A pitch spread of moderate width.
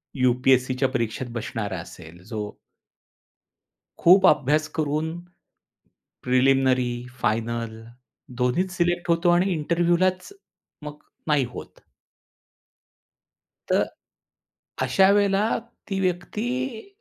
No: wide, 6.2 semitones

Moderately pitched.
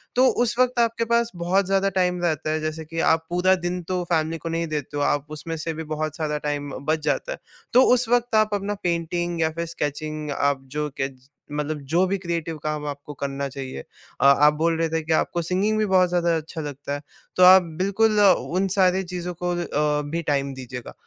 Yes: medium, 165 Hz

